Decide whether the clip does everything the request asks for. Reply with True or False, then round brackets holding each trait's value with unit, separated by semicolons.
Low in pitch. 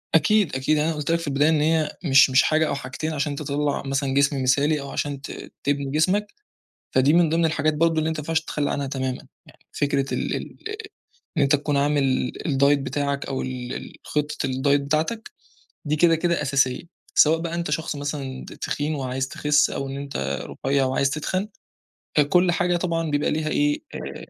False (145 Hz)